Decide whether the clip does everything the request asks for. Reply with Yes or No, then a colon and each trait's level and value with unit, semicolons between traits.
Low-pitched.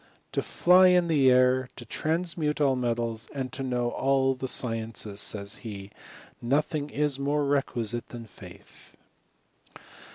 Yes: low, 130 Hz